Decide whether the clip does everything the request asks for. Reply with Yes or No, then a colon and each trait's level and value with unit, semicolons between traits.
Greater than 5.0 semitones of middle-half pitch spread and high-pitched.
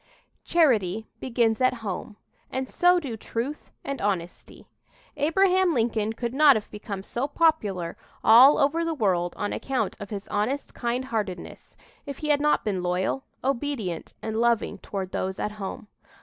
Yes: wide, 5.5 semitones; high, 230 Hz